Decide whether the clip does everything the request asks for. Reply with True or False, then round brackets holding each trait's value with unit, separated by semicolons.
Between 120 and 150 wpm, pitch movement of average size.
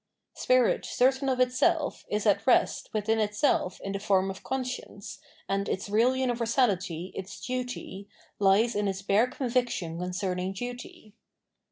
True (145 wpm; 4.4 semitones)